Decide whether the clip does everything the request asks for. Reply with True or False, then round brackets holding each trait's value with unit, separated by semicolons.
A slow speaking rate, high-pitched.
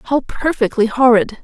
True (125 wpm; 240 Hz)